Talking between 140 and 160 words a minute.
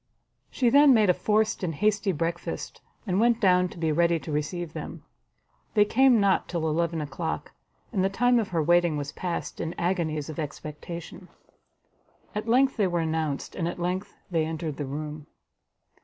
No: average, 175 wpm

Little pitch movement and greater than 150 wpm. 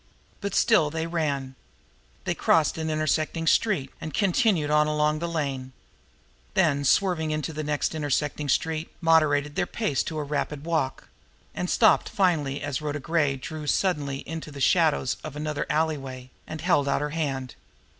Yes: narrow, 2.3 semitones; average, 165 wpm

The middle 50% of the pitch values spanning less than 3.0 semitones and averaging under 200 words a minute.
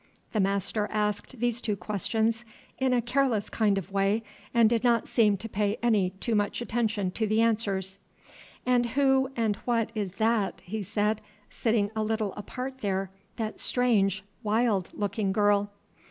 Yes: narrow, 2.5 semitones; average, 160 wpm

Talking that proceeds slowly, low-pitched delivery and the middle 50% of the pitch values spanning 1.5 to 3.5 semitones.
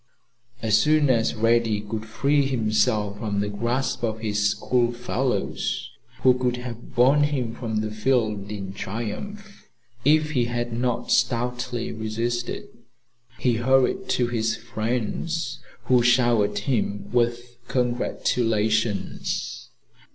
Yes: slow, 120 wpm; low, 120 Hz; narrow, 2.5 semitones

